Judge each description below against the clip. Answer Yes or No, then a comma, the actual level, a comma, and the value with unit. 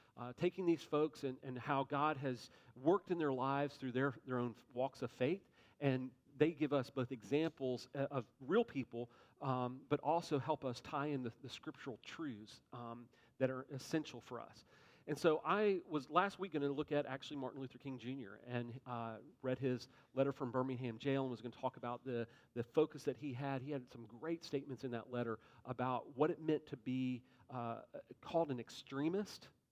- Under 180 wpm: No, average, 200 wpm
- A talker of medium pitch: No, low, 130 Hz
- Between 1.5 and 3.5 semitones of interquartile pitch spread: Yes, average, 2.8 semitones